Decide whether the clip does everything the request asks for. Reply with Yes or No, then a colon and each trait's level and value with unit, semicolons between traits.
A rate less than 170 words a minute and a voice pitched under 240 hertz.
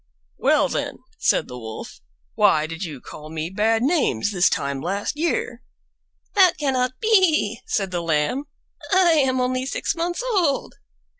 No: average, 150 wpm; high, 245 Hz